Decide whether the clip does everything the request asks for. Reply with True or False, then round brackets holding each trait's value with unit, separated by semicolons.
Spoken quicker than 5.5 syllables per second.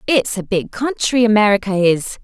False (4.9 syllables/s)